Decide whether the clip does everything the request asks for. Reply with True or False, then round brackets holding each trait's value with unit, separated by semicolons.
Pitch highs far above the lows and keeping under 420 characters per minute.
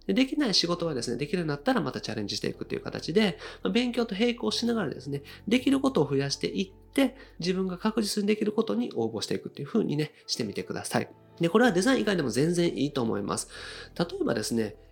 False (9.0 semitones; 495 characters per minute)